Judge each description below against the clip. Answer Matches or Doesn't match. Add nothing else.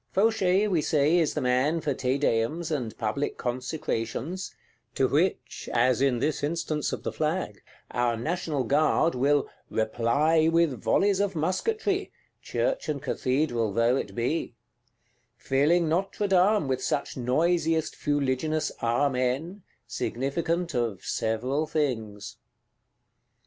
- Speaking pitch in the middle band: Matches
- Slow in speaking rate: Matches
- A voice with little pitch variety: Doesn't match